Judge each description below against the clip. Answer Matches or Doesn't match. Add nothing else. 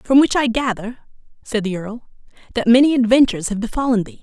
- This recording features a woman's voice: Matches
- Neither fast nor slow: Matches